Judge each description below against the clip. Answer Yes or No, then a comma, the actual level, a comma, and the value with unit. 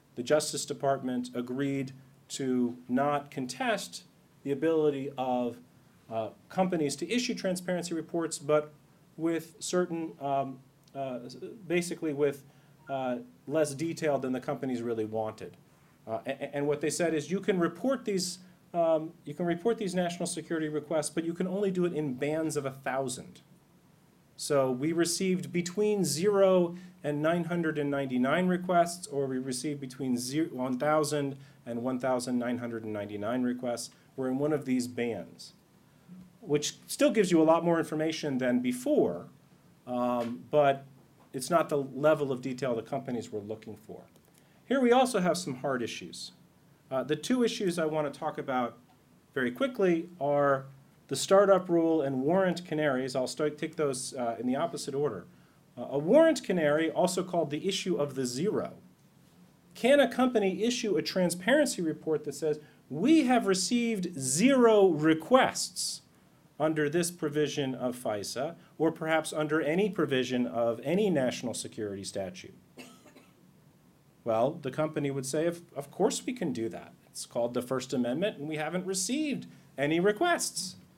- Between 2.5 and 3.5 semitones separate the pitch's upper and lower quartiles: No, average, 4.6 semitones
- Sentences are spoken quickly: No, average, 150 wpm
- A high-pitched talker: No, medium, 150 Hz